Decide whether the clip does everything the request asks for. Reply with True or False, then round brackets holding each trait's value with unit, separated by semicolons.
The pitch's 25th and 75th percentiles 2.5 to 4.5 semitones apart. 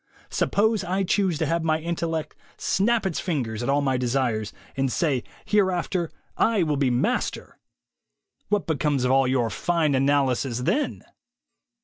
False (5.4 semitones)